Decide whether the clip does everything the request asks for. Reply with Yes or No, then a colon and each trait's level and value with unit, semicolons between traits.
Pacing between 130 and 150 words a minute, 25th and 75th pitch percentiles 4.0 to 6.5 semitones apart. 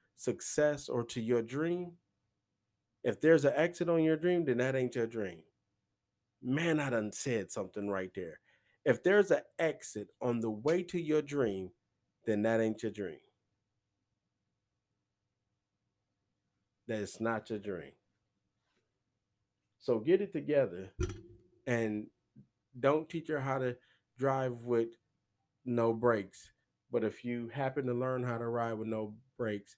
Yes: average, 140 wpm; average, 4.5 semitones